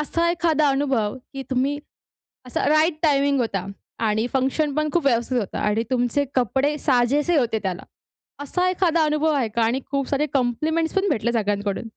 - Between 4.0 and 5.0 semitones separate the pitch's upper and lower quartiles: Yes, average, 4.4 semitones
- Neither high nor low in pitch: No, very high, 275 Hz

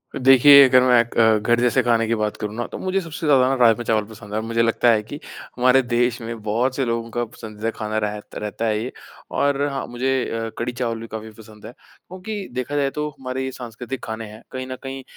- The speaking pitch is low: Yes, low, 120 Hz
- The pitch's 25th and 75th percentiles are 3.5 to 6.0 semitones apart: No, average, 2.9 semitones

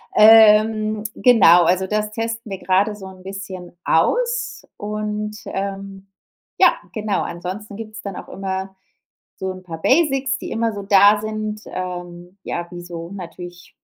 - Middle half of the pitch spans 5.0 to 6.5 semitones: No, average, 2.7 semitones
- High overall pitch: Yes, high, 200 Hz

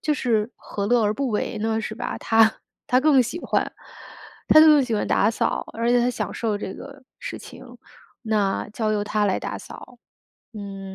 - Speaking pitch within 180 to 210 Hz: No, high, 225 Hz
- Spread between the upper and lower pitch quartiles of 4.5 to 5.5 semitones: No, average, 3.0 semitones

